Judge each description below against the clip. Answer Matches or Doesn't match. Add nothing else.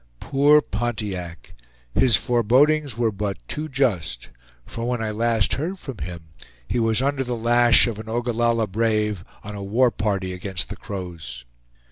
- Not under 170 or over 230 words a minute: Doesn't match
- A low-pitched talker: Matches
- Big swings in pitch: Doesn't match